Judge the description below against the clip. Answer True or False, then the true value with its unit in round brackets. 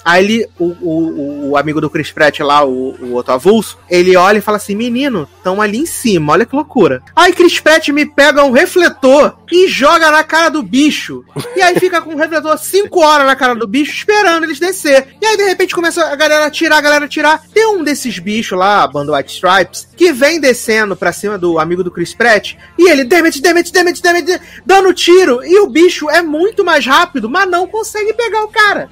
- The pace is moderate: False (220 wpm)